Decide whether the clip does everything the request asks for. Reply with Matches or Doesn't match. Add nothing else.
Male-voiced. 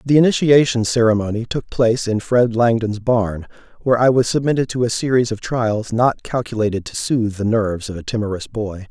Matches